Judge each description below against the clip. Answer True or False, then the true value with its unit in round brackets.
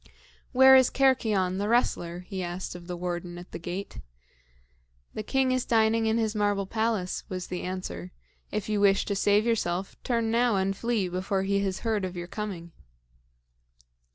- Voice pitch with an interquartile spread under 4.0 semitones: True (3.6 semitones)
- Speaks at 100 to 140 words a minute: False (175 wpm)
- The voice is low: False (200 Hz)